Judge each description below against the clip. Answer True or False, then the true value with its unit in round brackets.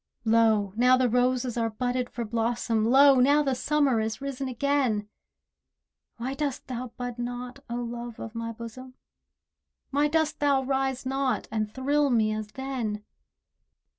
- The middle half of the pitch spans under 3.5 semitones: True (2.8 semitones)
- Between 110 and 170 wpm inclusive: True (150 wpm)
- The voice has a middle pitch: False (250 Hz)